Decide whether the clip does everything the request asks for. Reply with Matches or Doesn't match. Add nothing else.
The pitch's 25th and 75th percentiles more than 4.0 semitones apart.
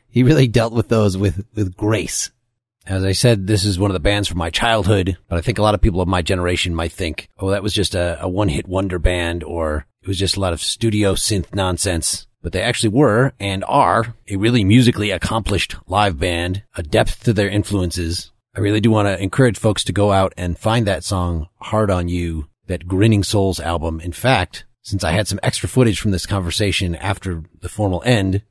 Doesn't match